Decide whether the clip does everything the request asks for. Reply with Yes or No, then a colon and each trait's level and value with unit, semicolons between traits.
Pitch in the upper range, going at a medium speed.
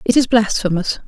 Yes: high, 215 Hz; average, 165 wpm